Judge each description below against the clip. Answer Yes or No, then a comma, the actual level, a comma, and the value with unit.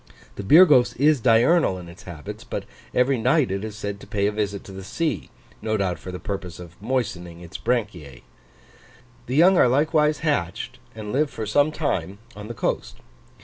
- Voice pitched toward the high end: No, low, 110 Hz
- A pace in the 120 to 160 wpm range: No, average, 190 wpm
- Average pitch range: No, wide, 6.5 semitones